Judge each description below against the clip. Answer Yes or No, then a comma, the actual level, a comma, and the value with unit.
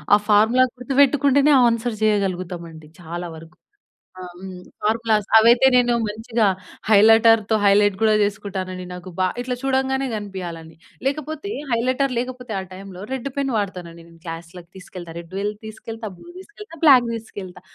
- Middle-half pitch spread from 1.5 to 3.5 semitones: No, average, 5.2 semitones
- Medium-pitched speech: No, high, 215 Hz